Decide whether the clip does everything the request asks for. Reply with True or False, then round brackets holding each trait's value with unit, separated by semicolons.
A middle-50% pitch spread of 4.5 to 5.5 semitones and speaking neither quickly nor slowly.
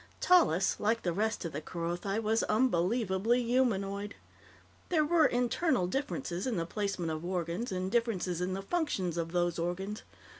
True (5.2 semitones; 155 wpm)